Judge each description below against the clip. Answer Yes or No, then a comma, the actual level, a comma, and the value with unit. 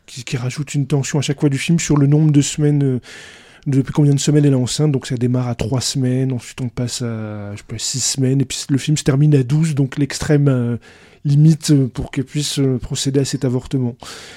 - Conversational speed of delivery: No, fast, 240 wpm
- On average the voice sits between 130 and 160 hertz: Yes, low, 135 Hz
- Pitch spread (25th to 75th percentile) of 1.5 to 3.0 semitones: Yes, average, 2.7 semitones